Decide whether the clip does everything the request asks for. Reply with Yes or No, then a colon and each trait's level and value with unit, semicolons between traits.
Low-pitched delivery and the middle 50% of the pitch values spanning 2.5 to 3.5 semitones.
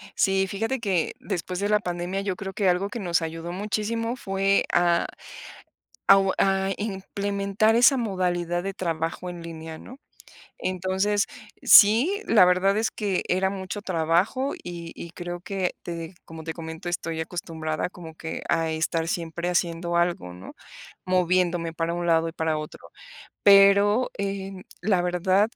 No: medium, 185 Hz; average, 2.8 semitones